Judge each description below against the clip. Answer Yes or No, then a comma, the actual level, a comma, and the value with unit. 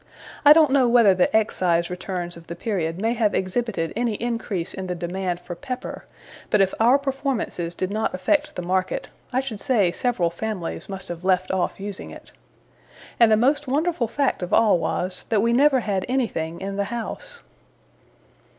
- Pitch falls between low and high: No, high, 205 Hz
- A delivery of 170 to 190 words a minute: Yes, average, 180 wpm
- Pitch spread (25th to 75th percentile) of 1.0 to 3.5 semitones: No, average, 5.2 semitones